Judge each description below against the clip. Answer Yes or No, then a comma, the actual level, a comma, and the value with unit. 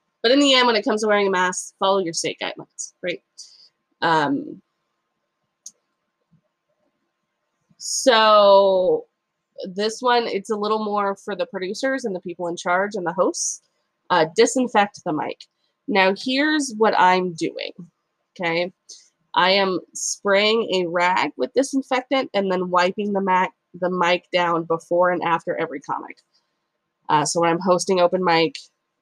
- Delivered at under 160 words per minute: Yes, average, 150 wpm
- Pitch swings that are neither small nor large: Yes, average, 3.6 semitones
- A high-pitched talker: Yes, high, 195 Hz